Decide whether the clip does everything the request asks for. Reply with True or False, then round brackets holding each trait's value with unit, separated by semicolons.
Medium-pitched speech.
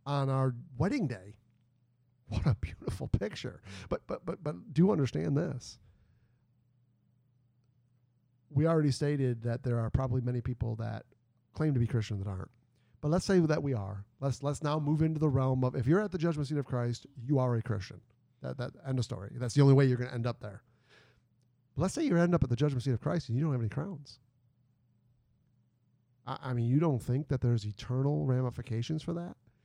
False (125 Hz)